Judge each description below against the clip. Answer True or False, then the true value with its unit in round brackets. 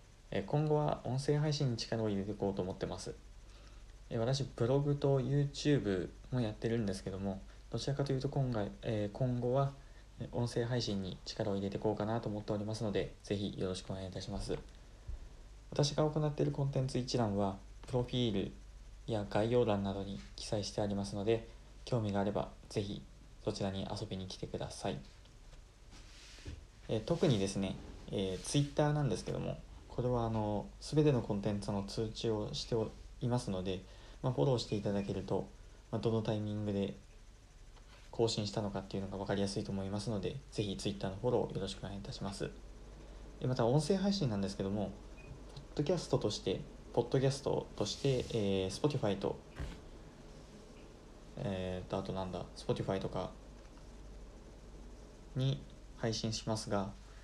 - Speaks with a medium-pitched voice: False (110 Hz)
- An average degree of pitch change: True (4.0 semitones)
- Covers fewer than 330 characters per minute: False (355 characters per minute)